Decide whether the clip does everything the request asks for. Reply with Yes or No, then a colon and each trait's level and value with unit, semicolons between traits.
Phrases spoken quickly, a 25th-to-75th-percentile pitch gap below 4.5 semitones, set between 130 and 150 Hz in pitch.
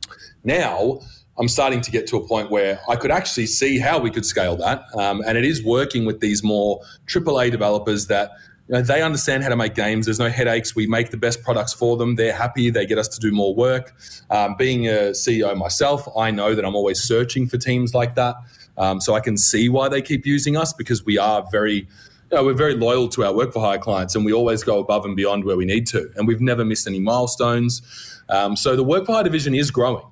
No: fast, 245 wpm; average, 3.0 semitones; low, 115 Hz